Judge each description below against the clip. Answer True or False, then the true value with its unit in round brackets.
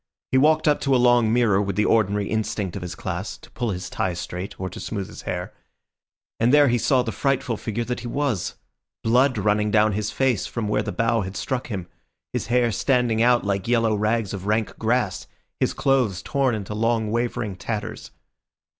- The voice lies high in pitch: False (110 Hz)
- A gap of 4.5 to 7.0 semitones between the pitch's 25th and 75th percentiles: False (3.4 semitones)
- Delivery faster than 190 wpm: True (200 wpm)